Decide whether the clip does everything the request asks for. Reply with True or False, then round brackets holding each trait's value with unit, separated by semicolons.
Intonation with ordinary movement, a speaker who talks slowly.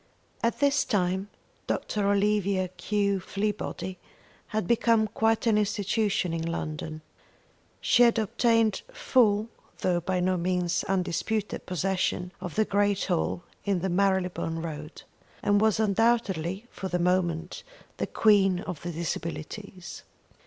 True (3.1 semitones; 125 wpm)